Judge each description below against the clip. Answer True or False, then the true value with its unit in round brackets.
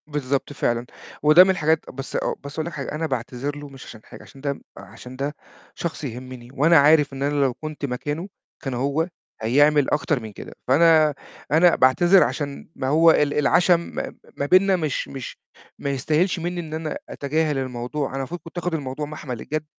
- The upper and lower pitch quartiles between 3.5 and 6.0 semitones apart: False (3.1 semitones)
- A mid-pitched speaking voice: True (145 Hz)